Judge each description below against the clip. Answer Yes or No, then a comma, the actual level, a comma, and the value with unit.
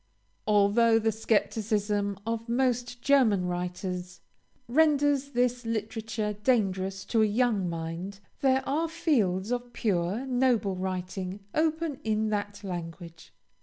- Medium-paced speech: No, slow, 115 wpm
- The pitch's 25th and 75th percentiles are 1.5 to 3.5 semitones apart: No, average, 4.5 semitones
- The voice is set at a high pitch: Yes, high, 215 Hz